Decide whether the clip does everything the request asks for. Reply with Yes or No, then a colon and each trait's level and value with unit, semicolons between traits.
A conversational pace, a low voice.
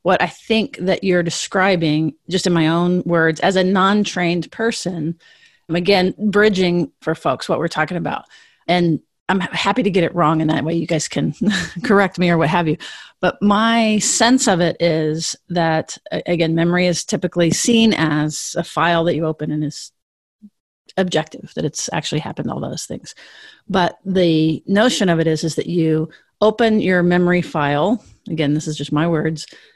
No: average, 180 wpm; medium, 175 Hz